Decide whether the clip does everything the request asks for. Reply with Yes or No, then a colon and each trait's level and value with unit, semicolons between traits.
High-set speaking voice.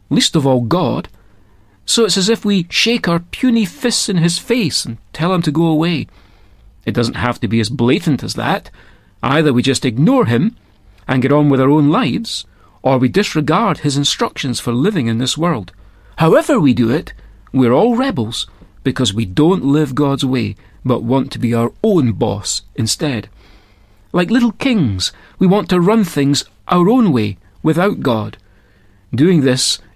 No: low, 130 Hz